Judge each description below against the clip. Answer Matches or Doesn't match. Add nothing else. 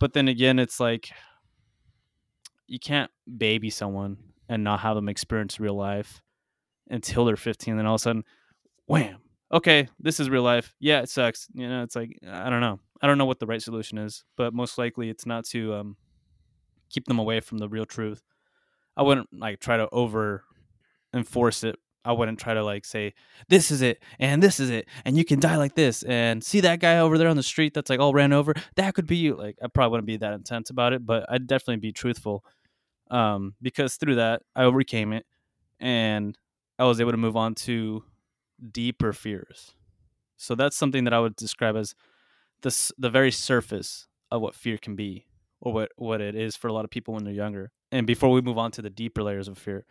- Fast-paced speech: Matches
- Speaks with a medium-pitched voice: Doesn't match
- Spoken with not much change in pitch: Doesn't match